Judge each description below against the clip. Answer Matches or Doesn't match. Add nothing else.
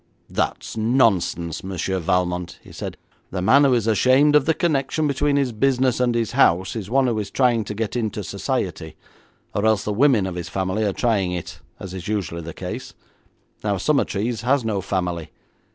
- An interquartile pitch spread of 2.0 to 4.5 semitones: Doesn't match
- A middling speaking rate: Matches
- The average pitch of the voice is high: Doesn't match